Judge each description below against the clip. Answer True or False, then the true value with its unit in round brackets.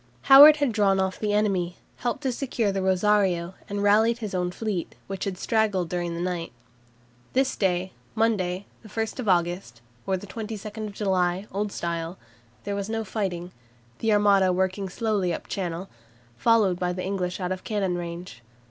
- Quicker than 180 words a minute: False (165 wpm)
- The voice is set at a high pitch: True (195 Hz)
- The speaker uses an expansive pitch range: False (3.1 semitones)